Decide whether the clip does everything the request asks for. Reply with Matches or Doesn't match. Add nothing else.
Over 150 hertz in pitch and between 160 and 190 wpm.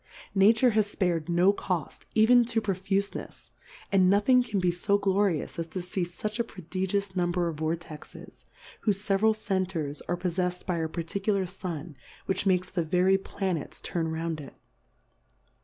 Matches